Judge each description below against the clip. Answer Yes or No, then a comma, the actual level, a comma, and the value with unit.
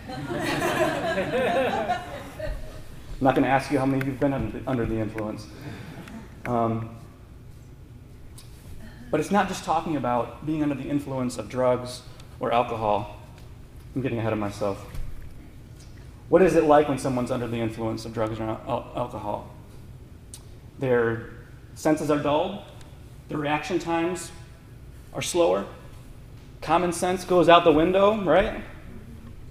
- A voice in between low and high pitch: No, low, 120 Hz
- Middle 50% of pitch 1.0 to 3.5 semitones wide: No, average, 4.0 semitones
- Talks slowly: Yes, slow, 130 wpm